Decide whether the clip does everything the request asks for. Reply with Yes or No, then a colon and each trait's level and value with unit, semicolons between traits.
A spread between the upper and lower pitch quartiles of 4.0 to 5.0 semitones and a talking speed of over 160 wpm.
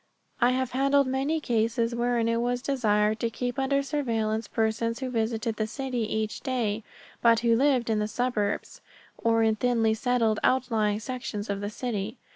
No: narrow, 2.6 semitones; average, 170 wpm